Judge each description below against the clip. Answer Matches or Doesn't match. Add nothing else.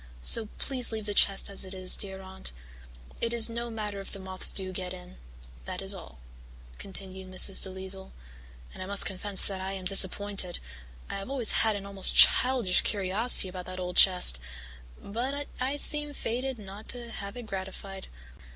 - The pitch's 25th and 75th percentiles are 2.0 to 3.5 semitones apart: Matches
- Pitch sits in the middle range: Doesn't match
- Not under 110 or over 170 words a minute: Doesn't match